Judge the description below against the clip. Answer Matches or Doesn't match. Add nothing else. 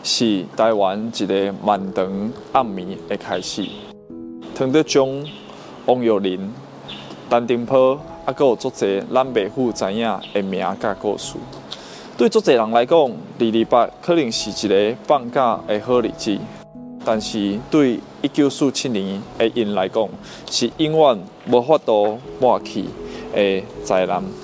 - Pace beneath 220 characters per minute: Matches